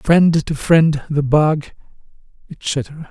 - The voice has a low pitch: No, medium, 155 Hz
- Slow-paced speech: Yes, slow, 115 wpm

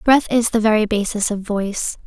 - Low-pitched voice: No, high, 215 Hz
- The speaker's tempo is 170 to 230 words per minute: Yes, fast, 205 wpm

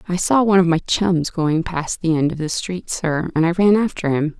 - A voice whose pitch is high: No, medium, 170 Hz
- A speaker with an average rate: No, fast, 260 wpm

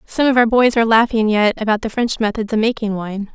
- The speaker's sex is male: No, female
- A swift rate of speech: Yes, fast, 250 wpm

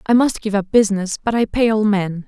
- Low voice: No, high, 210 Hz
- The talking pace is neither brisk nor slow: No, fast, 265 wpm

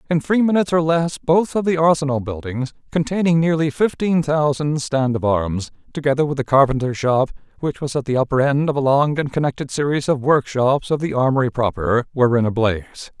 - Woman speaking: No, male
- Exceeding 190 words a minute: Yes, average, 200 wpm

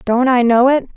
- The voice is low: No, very high, 250 Hz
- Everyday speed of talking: No, fast, 250 wpm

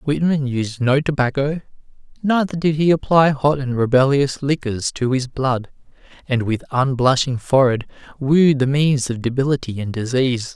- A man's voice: Yes, male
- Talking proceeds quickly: No, average, 150 wpm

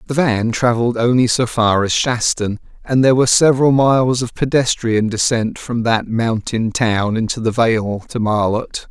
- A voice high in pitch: No, low, 115 Hz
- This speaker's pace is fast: No, average, 170 wpm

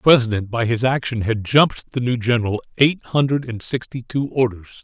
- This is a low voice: Yes, low, 120 Hz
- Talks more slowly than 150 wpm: No, average, 200 wpm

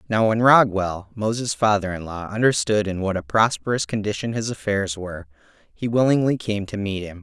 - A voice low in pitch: Yes, low, 105 Hz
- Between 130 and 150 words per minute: No, average, 185 wpm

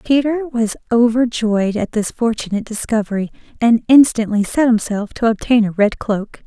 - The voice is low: No, high, 225 Hz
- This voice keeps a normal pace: Yes, average, 150 wpm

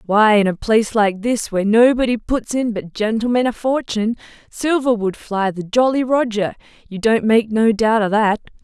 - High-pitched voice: Yes, high, 220 Hz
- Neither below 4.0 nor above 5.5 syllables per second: Yes, 5.0 syllables/s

